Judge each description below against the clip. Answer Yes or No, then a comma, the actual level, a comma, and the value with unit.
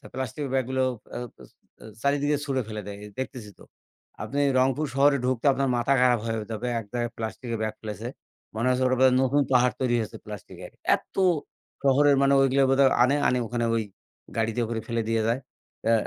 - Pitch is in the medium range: No, low, 125 Hz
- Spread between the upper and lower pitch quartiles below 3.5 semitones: Yes, average, 2.9 semitones